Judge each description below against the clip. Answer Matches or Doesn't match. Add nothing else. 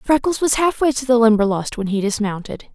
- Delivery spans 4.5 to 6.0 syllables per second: Matches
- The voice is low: Doesn't match